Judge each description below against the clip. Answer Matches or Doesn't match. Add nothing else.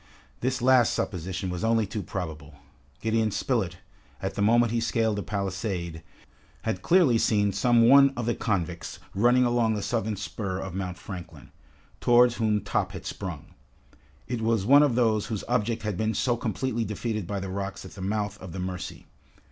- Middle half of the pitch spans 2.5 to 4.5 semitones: Matches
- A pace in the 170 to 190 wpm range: Matches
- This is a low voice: Matches